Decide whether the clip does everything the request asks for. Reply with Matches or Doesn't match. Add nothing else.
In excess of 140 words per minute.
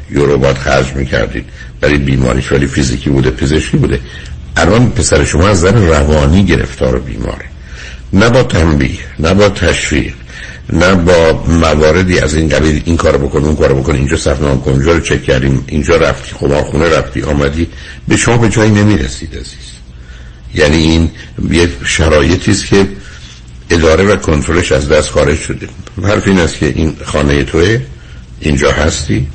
Matches